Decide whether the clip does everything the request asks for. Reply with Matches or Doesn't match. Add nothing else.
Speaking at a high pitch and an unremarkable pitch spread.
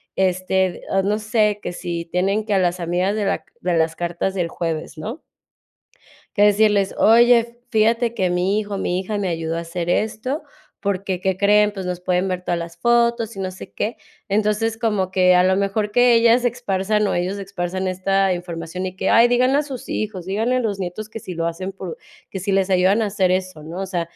Matches